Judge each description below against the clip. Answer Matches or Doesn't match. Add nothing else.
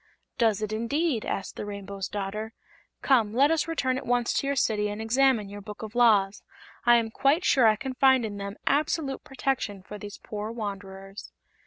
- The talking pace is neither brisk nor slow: Matches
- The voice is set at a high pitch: Matches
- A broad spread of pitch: Doesn't match